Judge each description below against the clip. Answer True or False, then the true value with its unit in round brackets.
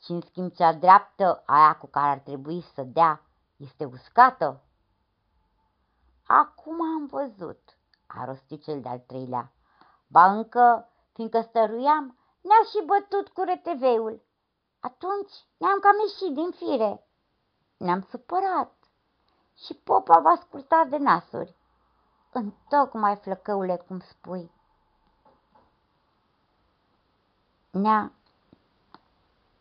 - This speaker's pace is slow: True (105 wpm)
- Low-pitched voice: False (220 Hz)